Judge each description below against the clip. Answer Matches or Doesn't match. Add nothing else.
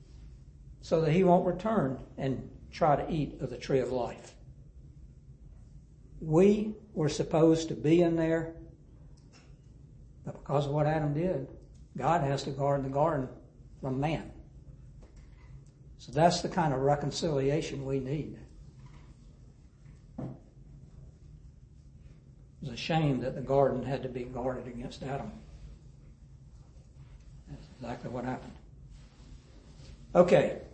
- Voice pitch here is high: Doesn't match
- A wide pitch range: Doesn't match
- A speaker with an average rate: Doesn't match